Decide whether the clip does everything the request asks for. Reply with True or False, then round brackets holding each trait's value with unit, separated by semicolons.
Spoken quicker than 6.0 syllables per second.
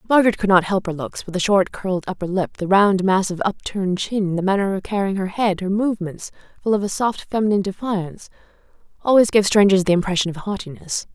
True (6.3 syllables/s)